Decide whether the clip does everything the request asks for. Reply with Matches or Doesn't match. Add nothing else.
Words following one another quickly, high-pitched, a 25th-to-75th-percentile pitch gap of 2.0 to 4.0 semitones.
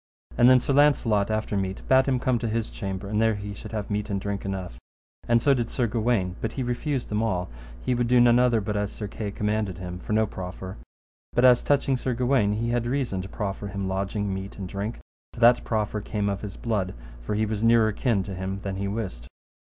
Doesn't match